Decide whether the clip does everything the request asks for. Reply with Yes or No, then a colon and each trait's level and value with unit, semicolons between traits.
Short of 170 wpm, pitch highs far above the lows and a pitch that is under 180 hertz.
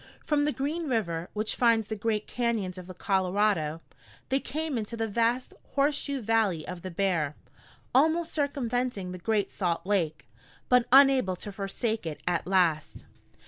No: average, 155 wpm; wide, 5.7 semitones; high, 215 Hz